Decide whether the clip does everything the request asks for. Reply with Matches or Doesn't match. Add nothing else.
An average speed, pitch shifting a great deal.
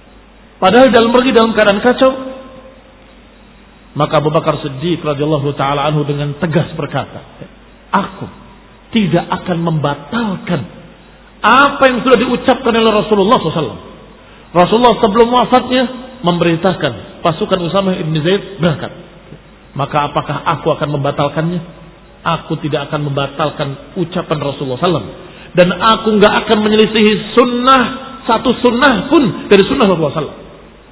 Matches